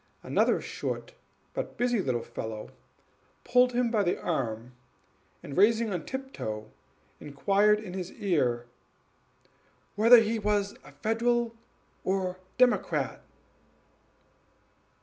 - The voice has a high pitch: Yes, high, 205 Hz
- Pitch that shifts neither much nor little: No, wide, 7.2 semitones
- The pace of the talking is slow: Yes, slow, 100 wpm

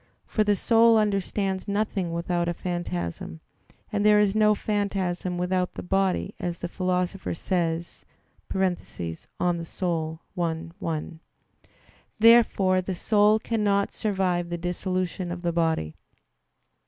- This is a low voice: No, medium, 185 Hz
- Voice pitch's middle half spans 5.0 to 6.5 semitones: No, average, 2.8 semitones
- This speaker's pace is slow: Yes, slow, 120 wpm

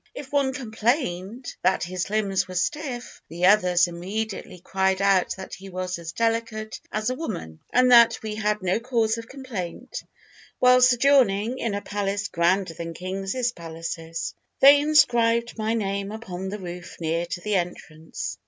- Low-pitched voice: No, high, 205 Hz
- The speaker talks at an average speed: Yes, average, 160 wpm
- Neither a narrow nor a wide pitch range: Yes, average, 4.4 semitones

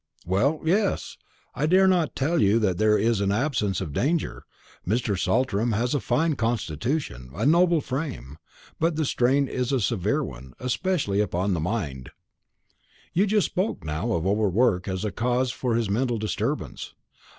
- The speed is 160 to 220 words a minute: Yes, average, 165 wpm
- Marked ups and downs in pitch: Yes, wide, 6.5 semitones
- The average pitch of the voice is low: Yes, low, 115 Hz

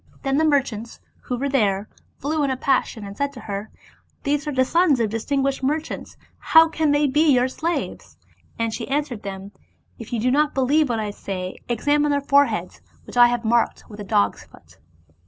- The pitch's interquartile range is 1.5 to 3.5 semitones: No, average, 4.6 semitones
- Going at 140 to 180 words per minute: No, fast, 205 wpm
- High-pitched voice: Yes, very high, 265 Hz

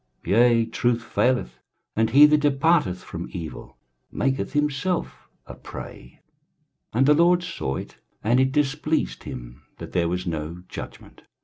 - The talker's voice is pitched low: Yes, low, 125 Hz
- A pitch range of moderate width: No, wide, 8.7 semitones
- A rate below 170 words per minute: Yes, average, 145 wpm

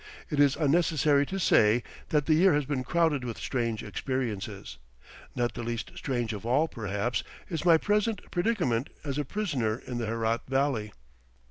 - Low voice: Yes, low, 130 Hz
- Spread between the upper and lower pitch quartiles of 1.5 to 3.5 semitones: No, average, 5.3 semitones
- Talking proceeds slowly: No, average, 165 wpm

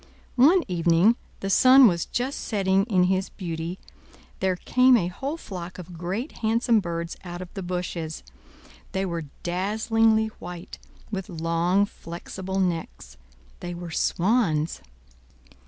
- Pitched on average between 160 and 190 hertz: Yes, medium, 185 Hz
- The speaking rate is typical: No, slow, 120 wpm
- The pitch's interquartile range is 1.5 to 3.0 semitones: No, average, 4.2 semitones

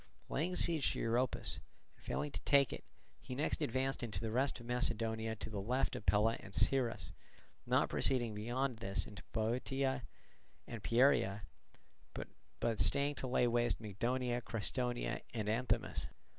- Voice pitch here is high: No, low, 120 Hz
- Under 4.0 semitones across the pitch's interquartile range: Yes, average, 2.9 semitones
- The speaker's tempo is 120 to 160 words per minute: Yes, average, 150 wpm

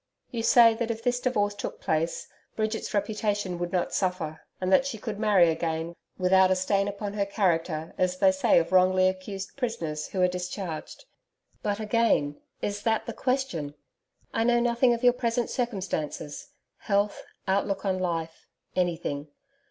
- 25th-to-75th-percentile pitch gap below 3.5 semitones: No, average, 4.2 semitones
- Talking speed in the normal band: Yes, average, 160 wpm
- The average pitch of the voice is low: No, high, 195 Hz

